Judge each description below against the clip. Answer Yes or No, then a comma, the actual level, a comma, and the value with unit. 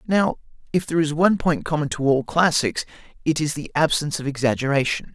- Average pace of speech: Yes, average, 185 wpm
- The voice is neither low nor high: Yes, medium, 150 Hz